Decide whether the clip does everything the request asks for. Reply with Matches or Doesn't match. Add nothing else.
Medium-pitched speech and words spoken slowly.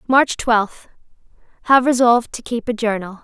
Doesn't match